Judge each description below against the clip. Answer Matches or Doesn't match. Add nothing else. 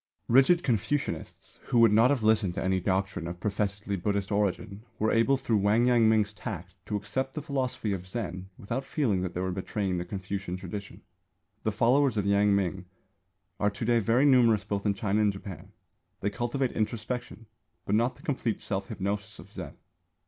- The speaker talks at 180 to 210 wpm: Matches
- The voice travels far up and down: Doesn't match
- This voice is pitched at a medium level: Doesn't match